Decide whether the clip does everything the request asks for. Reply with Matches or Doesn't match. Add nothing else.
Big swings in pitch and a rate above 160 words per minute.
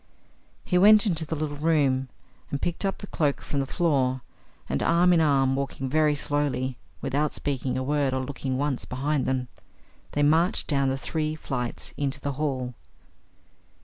Doesn't match